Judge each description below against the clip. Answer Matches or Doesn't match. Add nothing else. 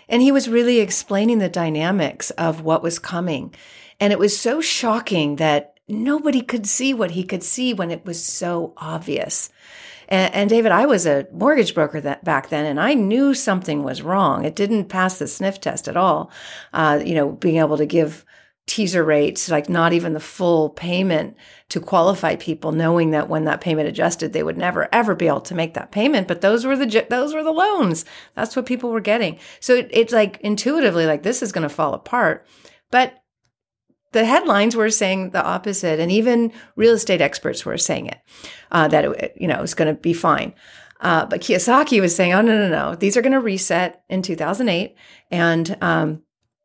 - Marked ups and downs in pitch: Matches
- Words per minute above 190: Matches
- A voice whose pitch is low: Doesn't match